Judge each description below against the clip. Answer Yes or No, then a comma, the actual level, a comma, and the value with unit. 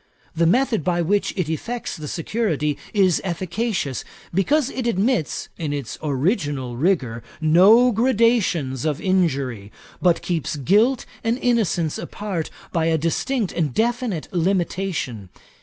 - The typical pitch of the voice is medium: Yes, medium, 175 Hz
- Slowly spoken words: Yes, slow, 125 wpm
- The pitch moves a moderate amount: No, wide, 6.7 semitones